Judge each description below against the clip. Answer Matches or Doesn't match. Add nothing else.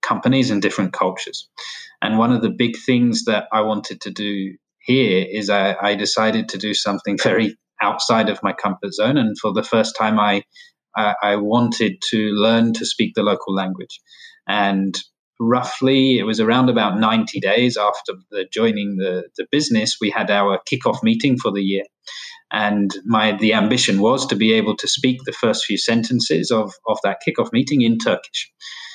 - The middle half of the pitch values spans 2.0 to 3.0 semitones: Doesn't match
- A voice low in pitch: Matches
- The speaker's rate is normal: Matches